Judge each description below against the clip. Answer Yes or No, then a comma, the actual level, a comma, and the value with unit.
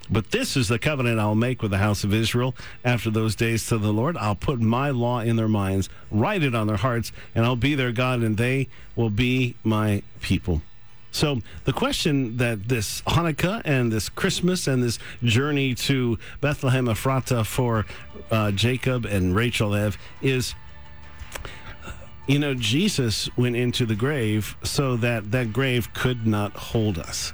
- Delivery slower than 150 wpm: No, average, 170 wpm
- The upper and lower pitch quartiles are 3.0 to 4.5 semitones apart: Yes, average, 3.4 semitones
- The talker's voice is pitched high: No, low, 120 Hz